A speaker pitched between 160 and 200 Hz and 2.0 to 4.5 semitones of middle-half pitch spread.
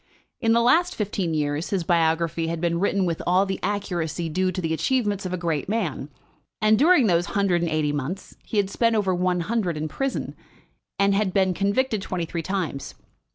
Yes: medium, 185 Hz; average, 3.5 semitones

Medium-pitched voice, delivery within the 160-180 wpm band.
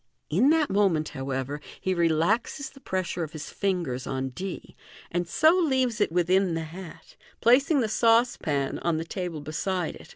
Yes: medium, 180 Hz; average, 170 wpm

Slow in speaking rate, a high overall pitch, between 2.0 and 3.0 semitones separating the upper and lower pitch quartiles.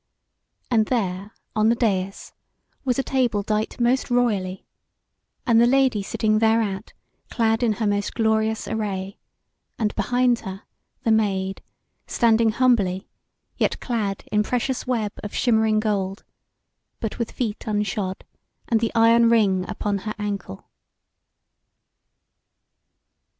Yes: slow, 125 wpm; high, 220 Hz; narrow, 2.5 semitones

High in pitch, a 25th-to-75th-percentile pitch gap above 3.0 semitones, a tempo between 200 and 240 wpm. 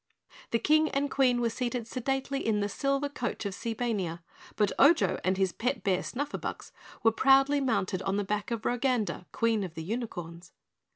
No: high, 230 Hz; average, 5.2 semitones; average, 175 wpm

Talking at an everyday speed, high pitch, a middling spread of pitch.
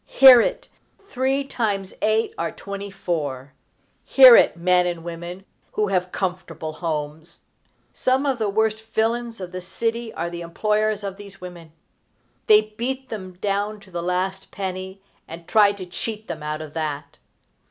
Yes: average, 160 wpm; high, 195 Hz; average, 4.0 semitones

